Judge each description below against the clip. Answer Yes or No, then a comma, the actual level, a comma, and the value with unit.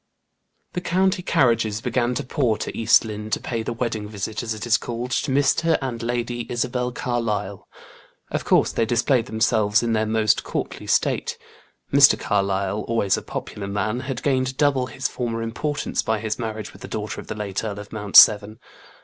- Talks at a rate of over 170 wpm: Yes, average, 185 wpm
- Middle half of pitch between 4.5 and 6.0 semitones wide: No, average, 2.8 semitones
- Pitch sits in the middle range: No, low, 115 Hz